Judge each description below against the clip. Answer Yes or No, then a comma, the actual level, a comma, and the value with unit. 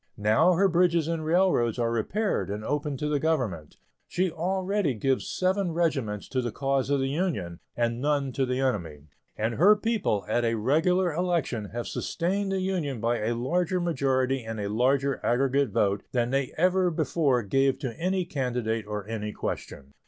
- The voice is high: No, low, 135 Hz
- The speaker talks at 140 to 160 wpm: No, average, 175 wpm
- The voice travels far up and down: Yes, wide, 6.8 semitones